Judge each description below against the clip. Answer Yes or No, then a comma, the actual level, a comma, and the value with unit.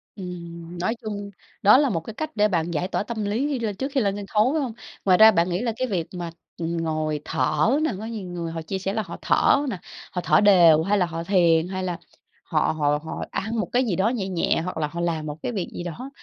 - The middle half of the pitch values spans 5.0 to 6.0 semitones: No, average, 4.6 semitones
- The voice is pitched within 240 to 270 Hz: No, medium, 185 Hz